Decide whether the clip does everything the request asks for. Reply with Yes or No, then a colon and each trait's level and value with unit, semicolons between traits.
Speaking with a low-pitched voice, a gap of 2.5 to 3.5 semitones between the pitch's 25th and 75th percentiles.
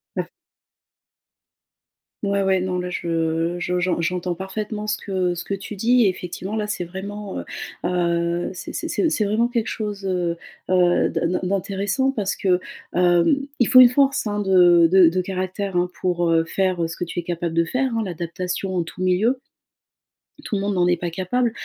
No: medium, 185 Hz; average, 2.9 semitones